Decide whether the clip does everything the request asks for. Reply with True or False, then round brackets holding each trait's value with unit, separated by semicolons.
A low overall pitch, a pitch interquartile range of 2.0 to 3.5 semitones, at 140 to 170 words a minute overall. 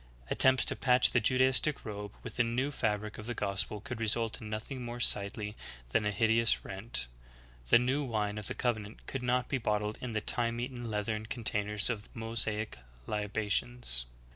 False (110 Hz; 2.6 semitones; 180 wpm)